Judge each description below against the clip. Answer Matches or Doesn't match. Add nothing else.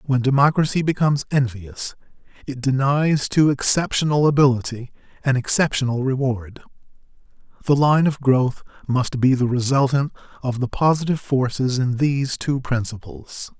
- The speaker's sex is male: Matches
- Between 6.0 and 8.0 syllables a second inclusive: Doesn't match